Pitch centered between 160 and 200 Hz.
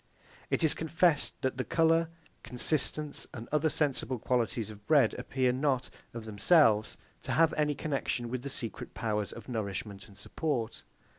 No: low, 130 Hz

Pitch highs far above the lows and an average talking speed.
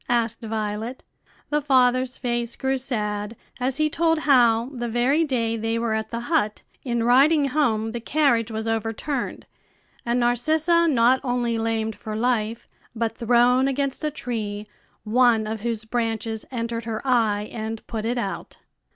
No: narrow, 2.6 semitones; average, 155 wpm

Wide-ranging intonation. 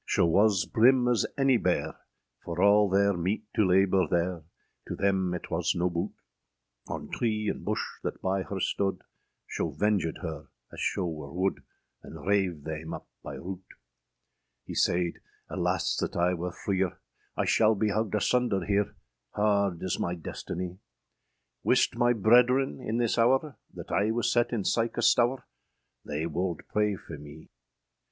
No: average, 3.9 semitones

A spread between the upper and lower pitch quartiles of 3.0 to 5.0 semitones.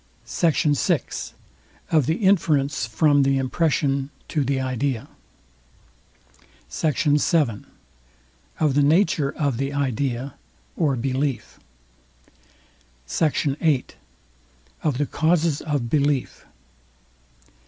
No: narrow, 2.5 semitones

